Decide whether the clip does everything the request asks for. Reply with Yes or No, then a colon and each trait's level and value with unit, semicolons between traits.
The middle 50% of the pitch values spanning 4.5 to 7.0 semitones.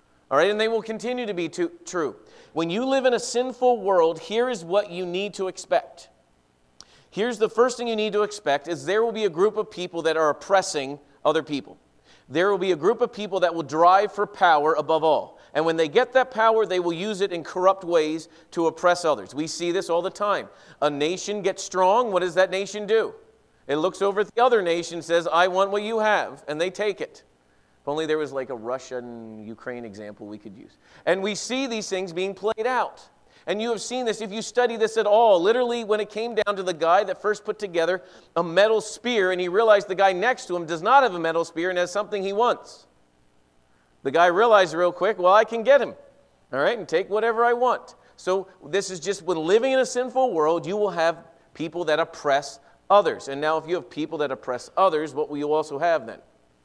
Yes: average, 5.1 semitones